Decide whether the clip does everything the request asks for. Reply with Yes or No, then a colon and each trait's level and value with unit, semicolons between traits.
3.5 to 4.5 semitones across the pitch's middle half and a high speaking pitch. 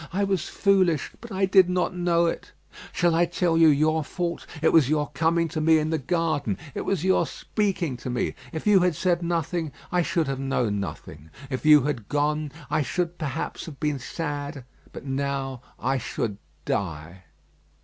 No: average, 4.1 semitones; medium, 155 Hz